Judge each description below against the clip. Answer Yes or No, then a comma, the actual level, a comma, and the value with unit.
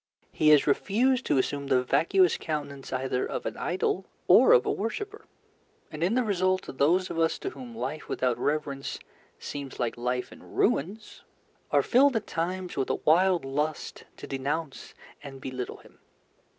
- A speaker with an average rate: Yes, average, 165 wpm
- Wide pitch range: Yes, wide, 5.9 semitones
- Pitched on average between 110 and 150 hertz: No, medium, 160 Hz